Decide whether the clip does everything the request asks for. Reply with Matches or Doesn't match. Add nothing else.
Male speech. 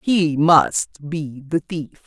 Doesn't match